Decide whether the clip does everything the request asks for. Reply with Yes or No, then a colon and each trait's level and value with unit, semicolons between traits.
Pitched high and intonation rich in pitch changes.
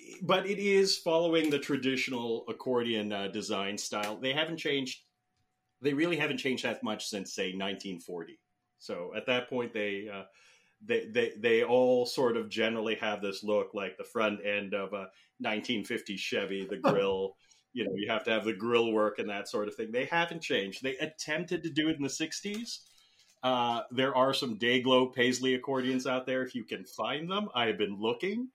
No: low, 130 Hz; wide, 6.8 semitones